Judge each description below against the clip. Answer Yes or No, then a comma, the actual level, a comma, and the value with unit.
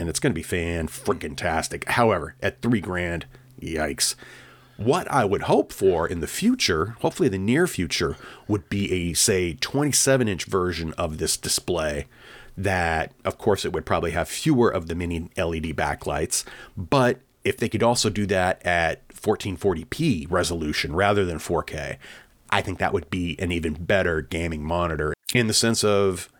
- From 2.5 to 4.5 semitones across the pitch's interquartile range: No, wide, 5.4 semitones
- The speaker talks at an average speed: Yes, average, 170 wpm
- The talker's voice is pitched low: Yes, very low, 90 Hz